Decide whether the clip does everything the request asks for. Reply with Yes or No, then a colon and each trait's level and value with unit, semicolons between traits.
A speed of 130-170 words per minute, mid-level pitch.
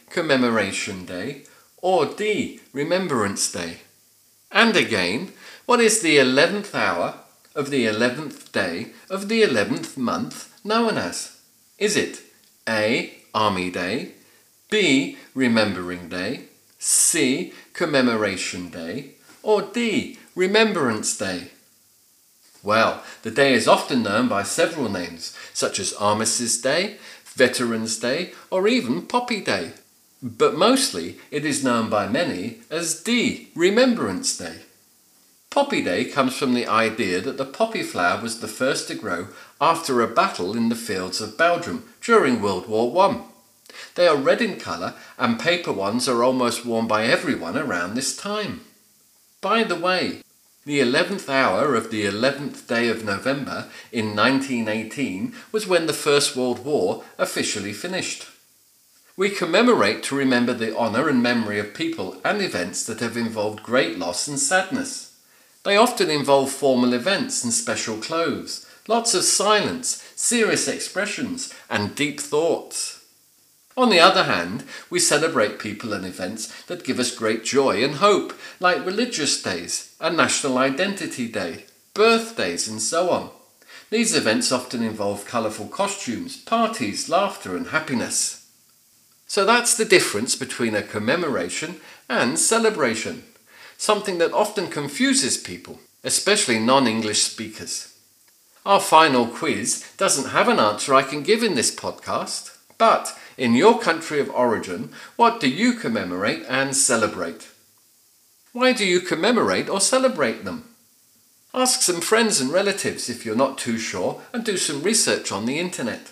Yes: average, 140 wpm; medium, 180 Hz